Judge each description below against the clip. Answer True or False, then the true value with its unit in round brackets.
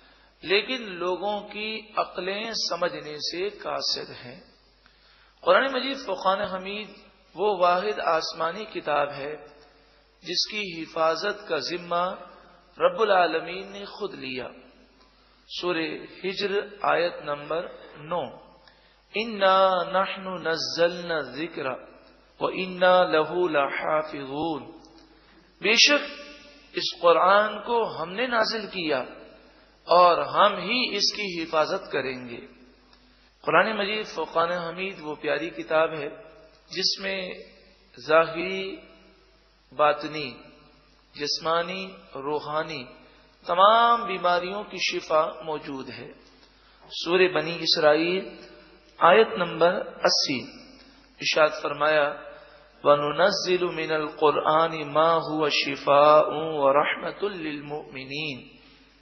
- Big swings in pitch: False (4.3 semitones)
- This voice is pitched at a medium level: True (175 Hz)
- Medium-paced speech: False (80 wpm)